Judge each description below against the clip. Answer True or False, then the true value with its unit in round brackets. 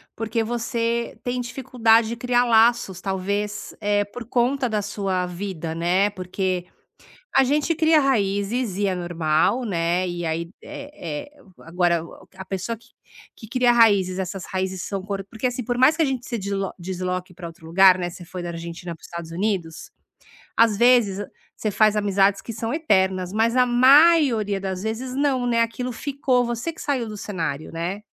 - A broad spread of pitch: False (4.8 semitones)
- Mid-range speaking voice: False (205 Hz)